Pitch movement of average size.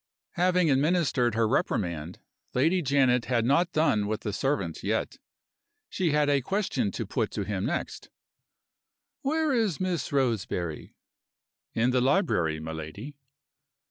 No: wide, 7.9 semitones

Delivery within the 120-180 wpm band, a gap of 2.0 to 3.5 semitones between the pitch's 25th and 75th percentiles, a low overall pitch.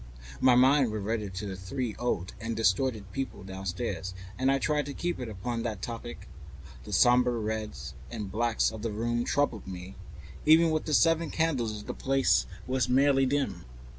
No: average, 170 wpm; average, 4.6 semitones; low, 120 Hz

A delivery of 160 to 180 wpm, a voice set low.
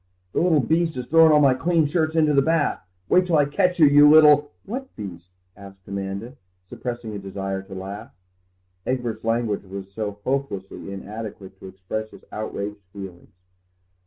Yes: average, 170 wpm; low, 115 Hz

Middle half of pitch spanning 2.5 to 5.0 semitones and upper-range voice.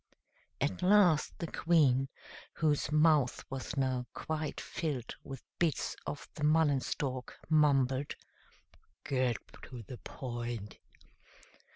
No: average, 3.3 semitones; medium, 140 Hz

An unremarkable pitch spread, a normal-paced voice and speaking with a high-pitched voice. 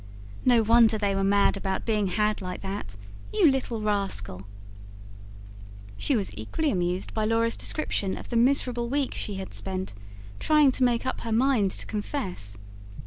Yes: average, 4.1 semitones; average, 160 wpm; high, 215 Hz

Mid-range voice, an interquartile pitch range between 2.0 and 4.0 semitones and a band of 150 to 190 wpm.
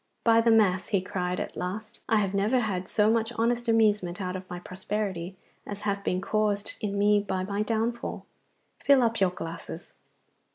No: high, 205 Hz; average, 3.1 semitones; average, 180 wpm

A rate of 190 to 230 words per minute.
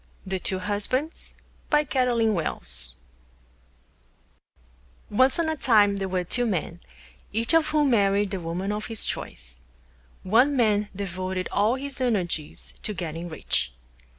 No: slow, 135 wpm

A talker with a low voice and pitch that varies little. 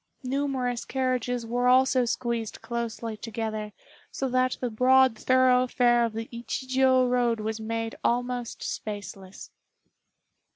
No: high, 245 Hz; narrow, 2.0 semitones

